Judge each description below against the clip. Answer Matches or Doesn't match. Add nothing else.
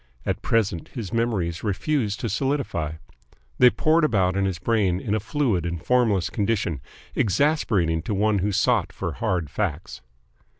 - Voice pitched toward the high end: Doesn't match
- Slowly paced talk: Doesn't match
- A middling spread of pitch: Matches